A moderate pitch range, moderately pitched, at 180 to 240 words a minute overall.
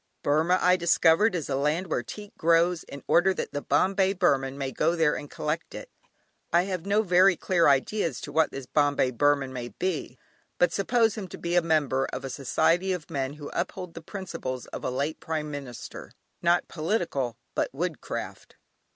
Yes: average, 4.3 semitones; medium, 160 Hz; average, 190 wpm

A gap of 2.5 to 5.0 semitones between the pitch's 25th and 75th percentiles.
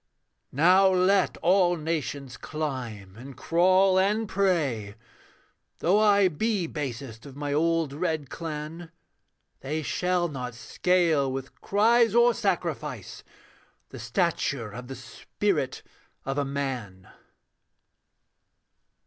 No: wide, 5.6 semitones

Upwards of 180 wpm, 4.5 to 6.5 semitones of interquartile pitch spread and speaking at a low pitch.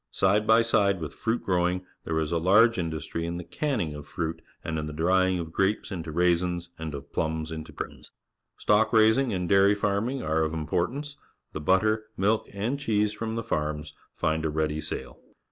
Yes: average, 195 wpm; average, 5.1 semitones; very low, 90 Hz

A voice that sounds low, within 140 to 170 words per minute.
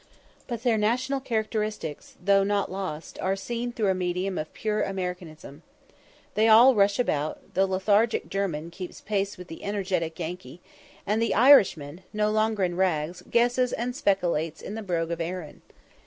No: high, 195 Hz; average, 160 wpm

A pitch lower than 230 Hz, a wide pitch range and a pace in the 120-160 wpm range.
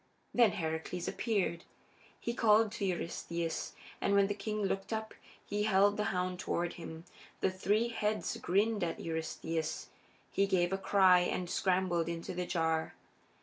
No: high, 190 Hz; average, 3.4 semitones; average, 150 wpm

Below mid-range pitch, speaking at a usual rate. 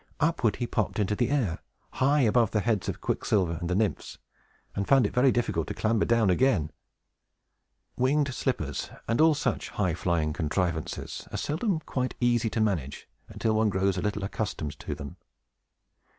Yes: low, 110 Hz; average, 170 wpm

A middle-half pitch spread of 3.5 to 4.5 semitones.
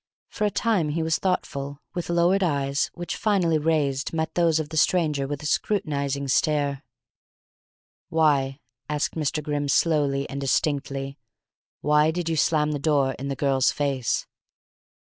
No: average, 2.7 semitones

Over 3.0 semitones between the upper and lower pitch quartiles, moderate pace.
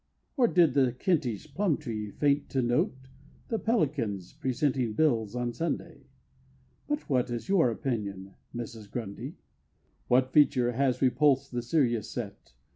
No: average, 4.2 semitones; slow, 130 wpm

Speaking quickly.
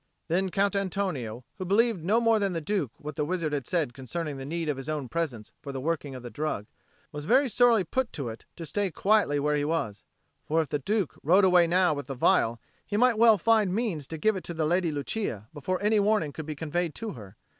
Yes: fast, 240 wpm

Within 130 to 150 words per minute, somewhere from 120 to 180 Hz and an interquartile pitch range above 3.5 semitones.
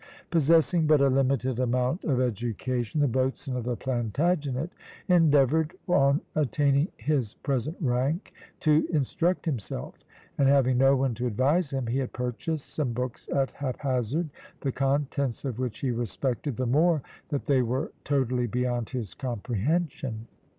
No: average, 145 wpm; low, 135 Hz; average, 3.0 semitones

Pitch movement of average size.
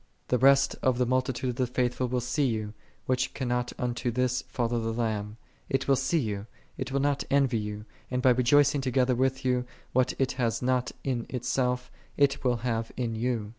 No: narrow, 1.7 semitones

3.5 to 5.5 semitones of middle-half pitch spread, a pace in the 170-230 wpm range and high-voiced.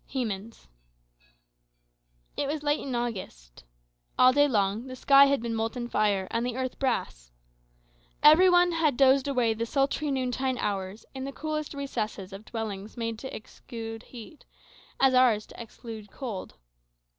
No: average, 4.1 semitones; average, 150 wpm; high, 240 Hz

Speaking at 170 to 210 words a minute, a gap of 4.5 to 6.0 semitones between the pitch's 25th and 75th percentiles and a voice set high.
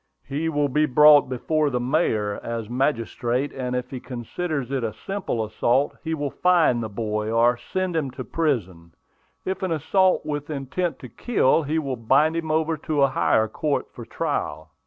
No: average, 180 wpm; average, 4.9 semitones; low, 135 Hz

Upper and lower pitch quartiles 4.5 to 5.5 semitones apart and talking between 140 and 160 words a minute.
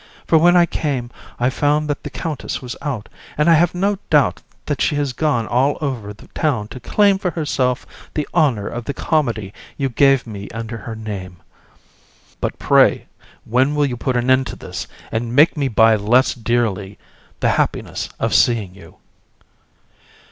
No: average, 4.9 semitones; average, 185 wpm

